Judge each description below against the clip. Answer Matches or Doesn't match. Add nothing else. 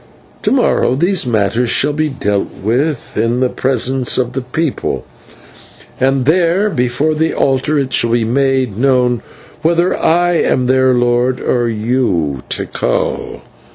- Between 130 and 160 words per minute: Matches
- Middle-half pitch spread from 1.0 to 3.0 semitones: Doesn't match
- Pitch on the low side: Matches